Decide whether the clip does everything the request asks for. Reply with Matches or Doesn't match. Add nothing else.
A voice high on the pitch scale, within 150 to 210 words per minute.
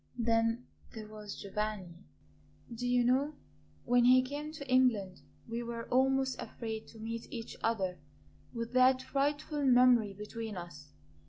Doesn't match